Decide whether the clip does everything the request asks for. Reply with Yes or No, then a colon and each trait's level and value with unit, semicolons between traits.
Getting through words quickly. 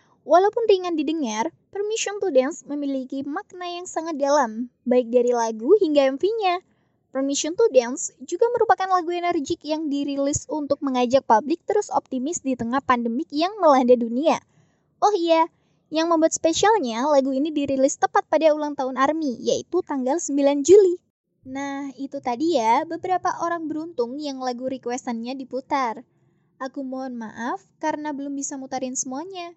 Yes: fast, 145 wpm